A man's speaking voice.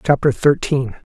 Yes: male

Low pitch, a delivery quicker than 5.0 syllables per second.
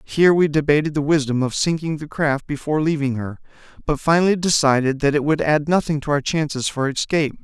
No: medium, 150 Hz; 6.0 syllables/s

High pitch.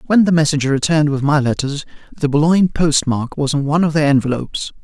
No: medium, 150 Hz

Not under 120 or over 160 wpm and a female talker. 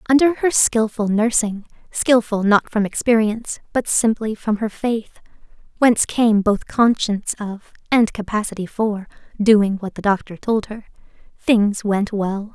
Yes: slow, 135 wpm; female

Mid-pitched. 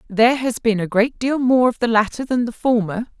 No: high, 235 Hz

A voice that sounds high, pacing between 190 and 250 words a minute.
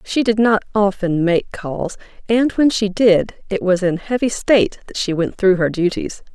Yes: high, 200 Hz; average, 200 wpm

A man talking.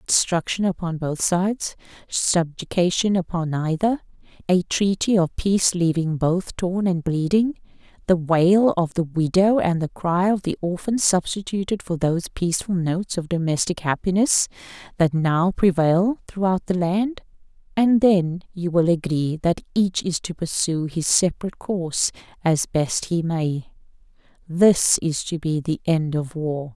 No: female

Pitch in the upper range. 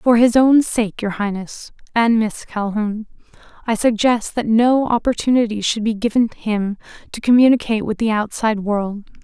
Yes: high, 225 Hz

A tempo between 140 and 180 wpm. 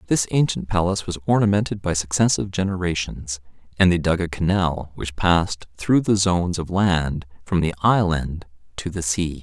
Yes: average, 165 wpm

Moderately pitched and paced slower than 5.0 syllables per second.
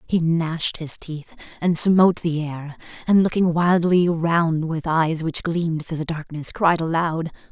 Yes: medium, 165 Hz; 4.2 syllables/s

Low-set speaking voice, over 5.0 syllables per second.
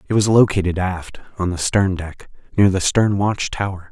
No: very low, 95 Hz; 4.9 syllables/s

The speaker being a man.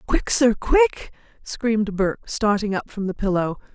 No: female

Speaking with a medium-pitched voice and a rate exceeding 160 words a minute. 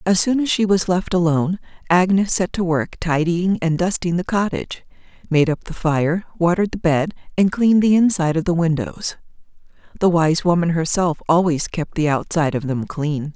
Yes: medium, 170 Hz; average, 185 wpm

